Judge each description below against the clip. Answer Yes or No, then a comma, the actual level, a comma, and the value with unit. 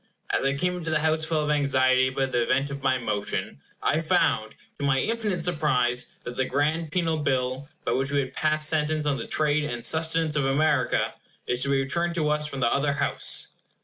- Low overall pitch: No, medium, 145 Hz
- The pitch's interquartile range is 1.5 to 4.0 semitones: Yes, average, 3.0 semitones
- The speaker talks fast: Yes, fast, 210 wpm